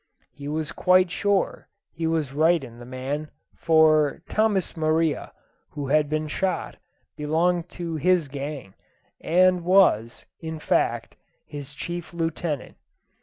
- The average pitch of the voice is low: No, medium, 160 Hz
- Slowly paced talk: Yes, slow, 125 wpm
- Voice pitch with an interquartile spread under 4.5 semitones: Yes, average, 3.2 semitones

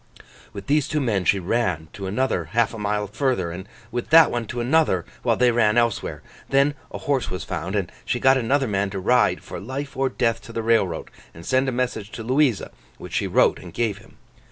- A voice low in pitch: Yes, low, 115 Hz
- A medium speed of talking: No, fast, 220 wpm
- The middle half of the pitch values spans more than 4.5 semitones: Yes, average, 4.9 semitones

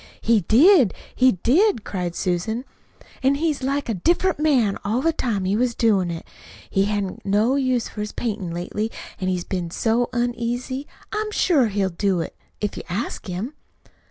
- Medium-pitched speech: No, high, 225 Hz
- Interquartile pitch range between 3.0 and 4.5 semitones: No, average, 5.2 semitones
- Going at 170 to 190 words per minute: Yes, average, 185 wpm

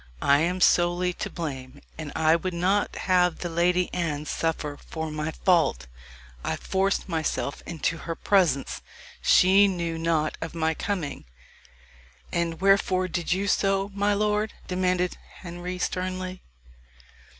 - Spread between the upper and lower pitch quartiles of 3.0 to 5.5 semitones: No, narrow, 2.4 semitones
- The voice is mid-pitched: Yes, medium, 175 Hz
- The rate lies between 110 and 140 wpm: Yes, slow, 135 wpm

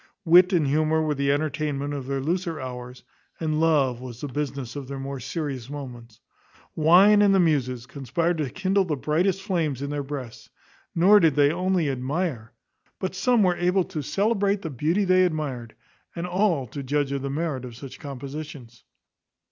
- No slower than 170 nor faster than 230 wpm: Yes, average, 180 wpm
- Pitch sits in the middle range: Yes, medium, 150 Hz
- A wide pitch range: No, average, 4.6 semitones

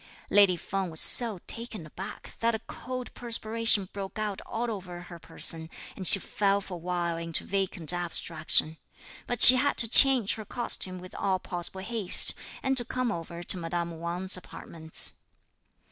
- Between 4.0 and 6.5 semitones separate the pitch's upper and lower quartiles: Yes, average, 4.7 semitones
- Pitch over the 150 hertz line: Yes, high, 190 Hz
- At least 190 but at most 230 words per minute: No, average, 165 wpm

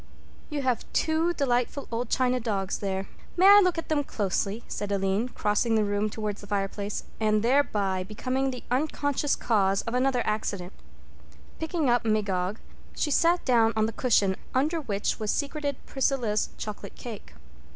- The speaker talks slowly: No, average, 160 wpm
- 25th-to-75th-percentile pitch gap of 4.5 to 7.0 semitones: Yes, average, 5.1 semitones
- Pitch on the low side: No, high, 230 Hz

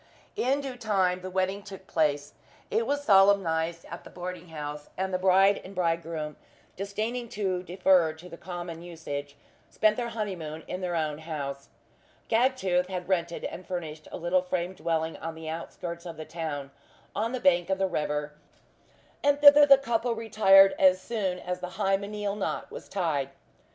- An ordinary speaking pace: Yes, average, 170 wpm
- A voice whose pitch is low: No, medium, 180 Hz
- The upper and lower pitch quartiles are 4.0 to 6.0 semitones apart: No, average, 3.5 semitones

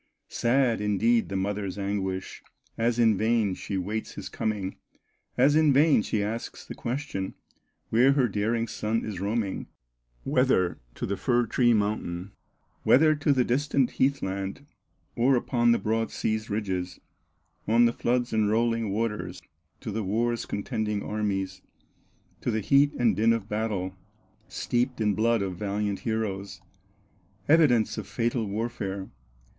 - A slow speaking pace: No, average, 145 wpm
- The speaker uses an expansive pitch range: No, average, 2.9 semitones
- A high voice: No, low, 110 Hz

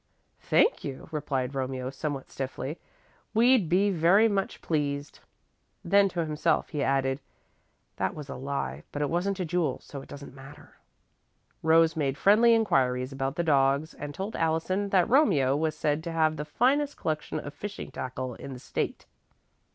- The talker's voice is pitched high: No, medium, 155 Hz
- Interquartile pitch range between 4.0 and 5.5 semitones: Yes, average, 5.2 semitones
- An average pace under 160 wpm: No, average, 165 wpm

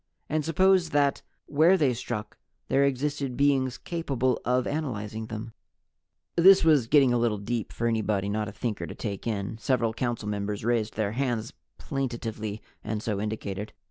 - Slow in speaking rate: No, average, 160 wpm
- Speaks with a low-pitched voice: Yes, low, 120 Hz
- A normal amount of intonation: Yes, average, 4.5 semitones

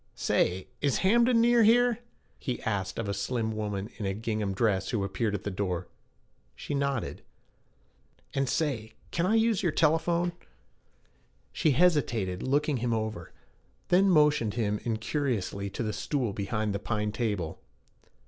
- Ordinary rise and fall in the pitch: No, wide, 6.7 semitones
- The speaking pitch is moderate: No, low, 115 Hz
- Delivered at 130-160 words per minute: Yes, average, 150 wpm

